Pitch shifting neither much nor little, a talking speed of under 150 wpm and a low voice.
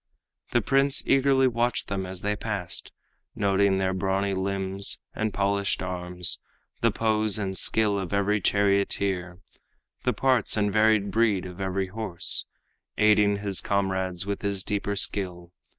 No: narrow, 2.0 semitones; average, 140 wpm; low, 100 Hz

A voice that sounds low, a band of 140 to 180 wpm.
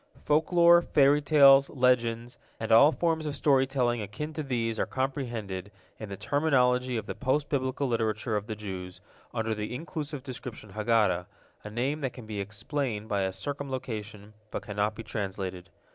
Yes: low, 120 Hz; average, 165 wpm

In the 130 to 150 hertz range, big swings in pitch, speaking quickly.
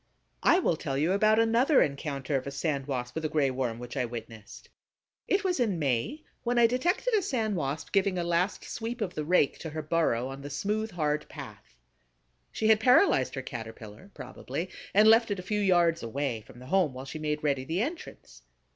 No: medium, 160 Hz; wide, 8.1 semitones; fast, 210 wpm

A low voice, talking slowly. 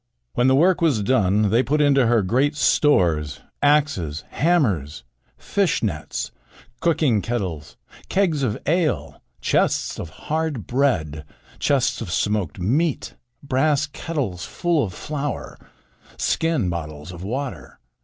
Yes: low, 130 Hz; slow, 125 wpm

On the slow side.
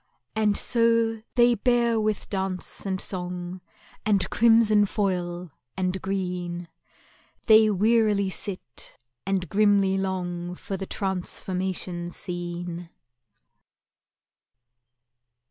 Yes: slow, 90 wpm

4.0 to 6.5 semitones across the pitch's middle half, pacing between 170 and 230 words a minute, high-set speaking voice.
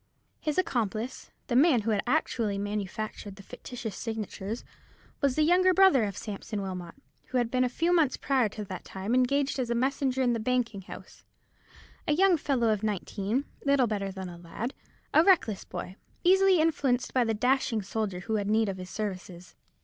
Yes: average, 5.0 semitones; average, 180 wpm; high, 230 Hz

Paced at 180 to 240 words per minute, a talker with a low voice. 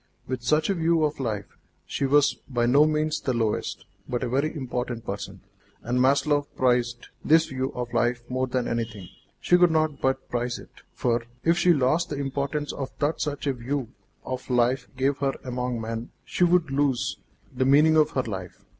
Yes: average, 185 wpm; low, 130 Hz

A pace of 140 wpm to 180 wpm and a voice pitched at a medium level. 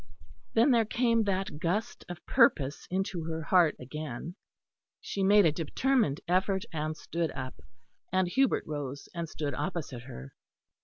Yes: average, 145 wpm; medium, 170 Hz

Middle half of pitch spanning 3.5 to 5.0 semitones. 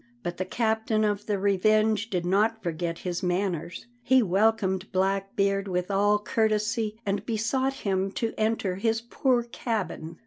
No: average, 2.8 semitones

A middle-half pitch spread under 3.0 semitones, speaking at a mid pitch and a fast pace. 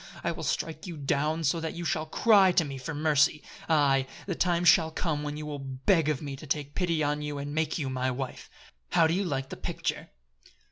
Yes: narrow, 2.6 semitones; medium, 150 Hz; fast, 230 wpm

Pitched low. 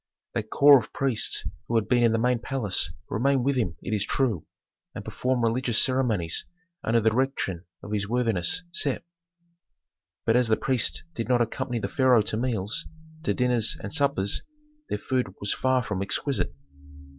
Yes: low, 120 Hz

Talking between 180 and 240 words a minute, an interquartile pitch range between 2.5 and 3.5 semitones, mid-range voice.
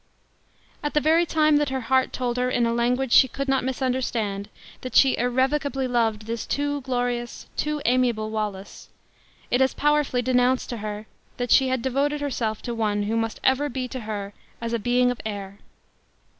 No: average, 185 wpm; average, 2.8 semitones; very high, 250 Hz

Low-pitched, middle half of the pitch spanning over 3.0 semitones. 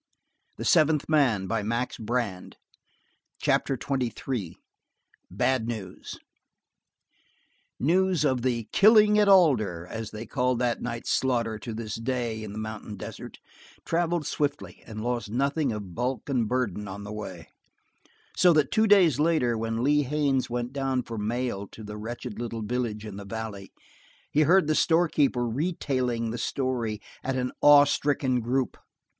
Yes: low, 125 Hz; average, 4.4 semitones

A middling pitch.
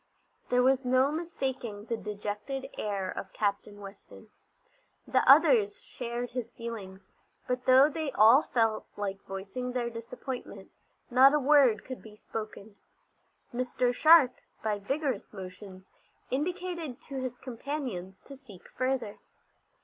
No: high, 245 Hz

